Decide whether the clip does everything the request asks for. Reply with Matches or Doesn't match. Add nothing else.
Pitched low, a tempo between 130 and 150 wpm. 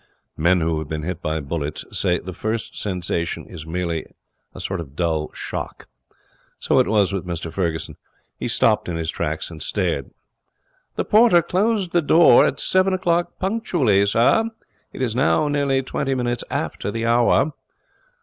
Doesn't match